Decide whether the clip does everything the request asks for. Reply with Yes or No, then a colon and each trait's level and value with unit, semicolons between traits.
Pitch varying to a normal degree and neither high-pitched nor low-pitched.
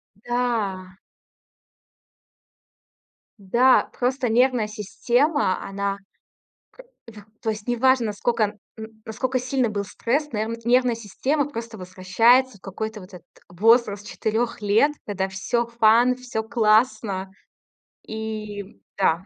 No: average, 3.2 semitones; high, 220 Hz